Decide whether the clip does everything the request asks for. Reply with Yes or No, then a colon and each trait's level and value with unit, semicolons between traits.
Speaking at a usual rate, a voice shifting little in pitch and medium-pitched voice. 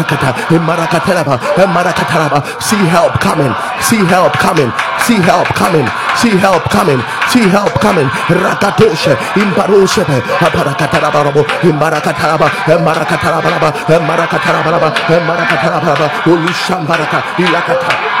No: slow, 115 wpm; narrow, 1.8 semitones; medium, 165 Hz